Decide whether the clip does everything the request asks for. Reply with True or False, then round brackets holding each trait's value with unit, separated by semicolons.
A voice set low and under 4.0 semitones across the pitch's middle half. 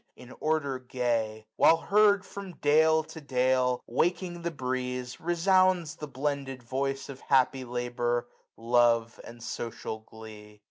False (130 Hz; 4.7 semitones)